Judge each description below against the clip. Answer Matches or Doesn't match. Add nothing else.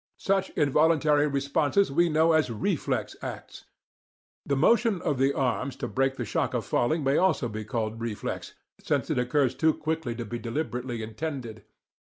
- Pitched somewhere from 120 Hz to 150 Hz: Matches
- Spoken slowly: Doesn't match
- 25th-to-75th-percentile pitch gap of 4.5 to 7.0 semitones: Matches